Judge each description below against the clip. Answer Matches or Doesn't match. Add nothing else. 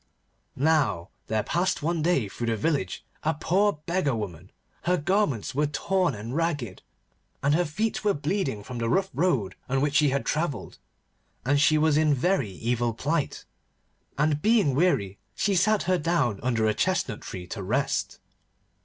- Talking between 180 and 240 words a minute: Doesn't match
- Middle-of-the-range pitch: Matches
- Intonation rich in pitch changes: Matches